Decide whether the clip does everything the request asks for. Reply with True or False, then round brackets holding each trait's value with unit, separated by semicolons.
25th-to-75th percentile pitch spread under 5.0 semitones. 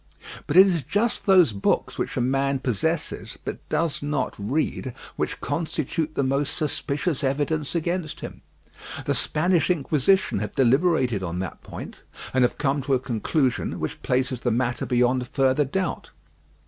True (4.0 semitones)